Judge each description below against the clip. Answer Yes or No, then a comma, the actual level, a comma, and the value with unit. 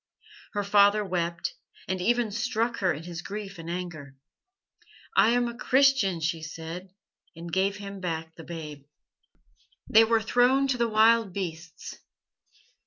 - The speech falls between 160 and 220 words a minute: No, average, 145 wpm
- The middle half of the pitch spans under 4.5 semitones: No, average, 5.2 semitones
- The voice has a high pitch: Yes, high, 195 Hz